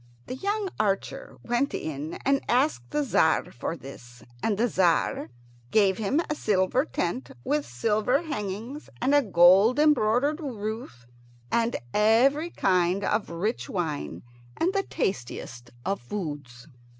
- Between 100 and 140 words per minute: Yes, slow, 135 wpm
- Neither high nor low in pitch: No, high, 210 Hz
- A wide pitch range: Yes, wide, 7.8 semitones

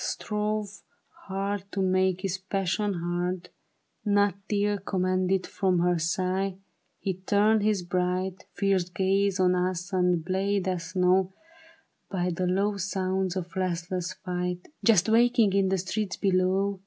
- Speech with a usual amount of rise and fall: No, narrow, 1.6 semitones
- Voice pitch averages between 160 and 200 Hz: Yes, high, 190 Hz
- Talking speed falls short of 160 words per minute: Yes, slow, 135 wpm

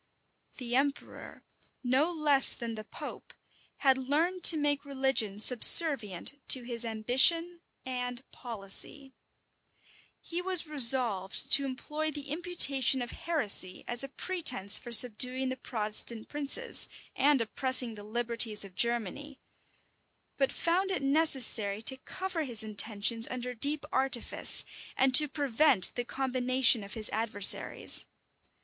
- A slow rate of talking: Yes, slow, 125 wpm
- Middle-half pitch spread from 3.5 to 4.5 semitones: Yes, average, 4.1 semitones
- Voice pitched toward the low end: No, very high, 260 Hz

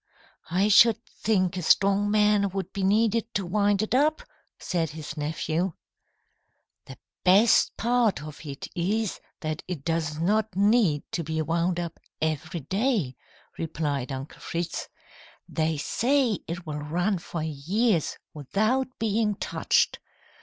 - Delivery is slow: Yes, slow, 130 wpm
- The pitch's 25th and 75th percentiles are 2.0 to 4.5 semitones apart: No, average, 5.1 semitones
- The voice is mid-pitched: Yes, medium, 180 Hz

